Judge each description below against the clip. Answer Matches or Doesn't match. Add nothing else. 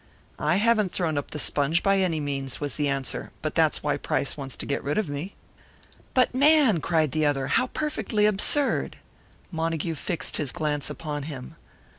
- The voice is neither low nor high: Matches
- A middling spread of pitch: Doesn't match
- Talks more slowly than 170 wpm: Doesn't match